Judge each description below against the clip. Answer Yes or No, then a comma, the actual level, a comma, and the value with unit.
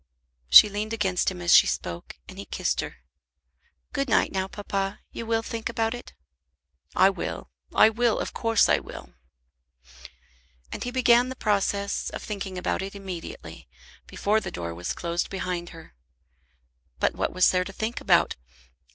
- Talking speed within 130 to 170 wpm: Yes, average, 165 wpm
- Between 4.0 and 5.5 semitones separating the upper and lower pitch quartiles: No, average, 3.6 semitones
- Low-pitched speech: No, high, 200 Hz